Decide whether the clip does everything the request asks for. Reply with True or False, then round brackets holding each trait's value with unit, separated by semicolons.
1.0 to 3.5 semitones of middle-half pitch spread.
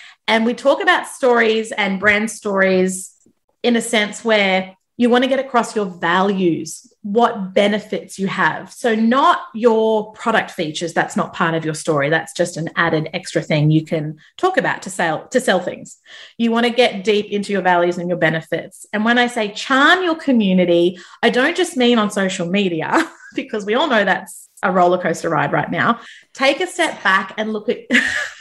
False (5.1 semitones)